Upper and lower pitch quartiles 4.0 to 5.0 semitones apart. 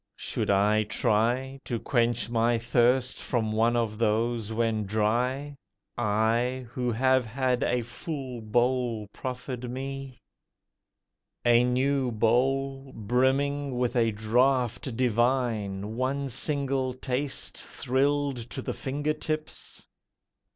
No: average, 2.7 semitones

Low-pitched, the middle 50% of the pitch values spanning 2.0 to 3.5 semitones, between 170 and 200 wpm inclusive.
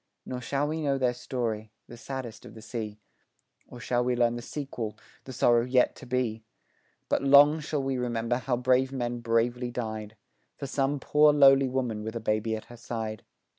Yes: low, 125 Hz; average, 2.8 semitones; average, 190 wpm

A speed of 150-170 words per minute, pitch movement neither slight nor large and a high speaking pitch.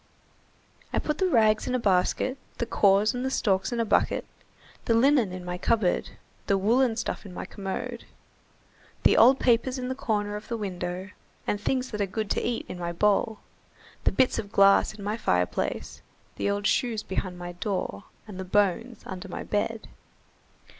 No: average, 180 wpm; average, 3.7 semitones; high, 210 Hz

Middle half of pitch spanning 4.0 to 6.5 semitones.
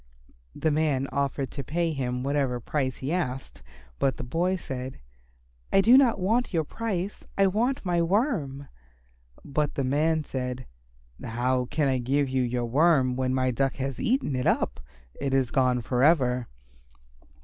Yes: average, 4.6 semitones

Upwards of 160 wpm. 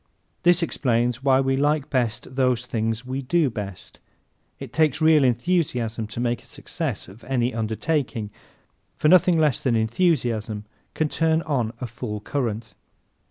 No: average, 150 wpm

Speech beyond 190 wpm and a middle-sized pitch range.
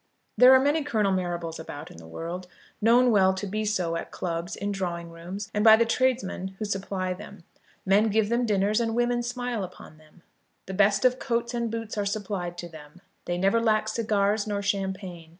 Yes: average, 200 wpm; average, 3.9 semitones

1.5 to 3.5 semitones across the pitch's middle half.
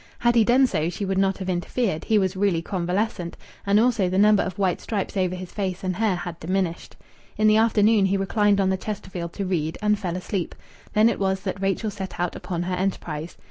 Yes: narrow, 2.5 semitones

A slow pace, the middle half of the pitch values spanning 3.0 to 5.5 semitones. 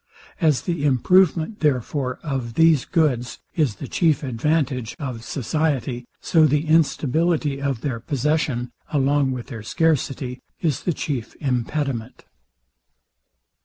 Yes: slow, 120 wpm; average, 3.8 semitones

